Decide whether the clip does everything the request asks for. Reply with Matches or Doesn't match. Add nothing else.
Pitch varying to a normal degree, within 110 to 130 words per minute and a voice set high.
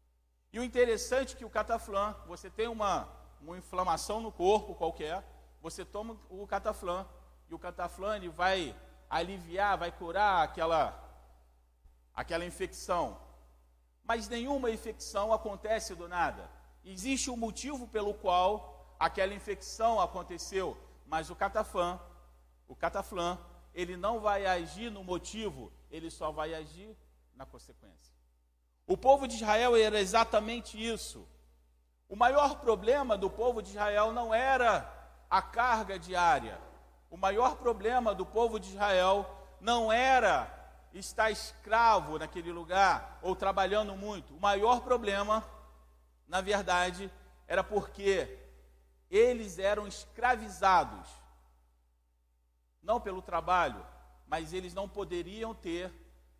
Matches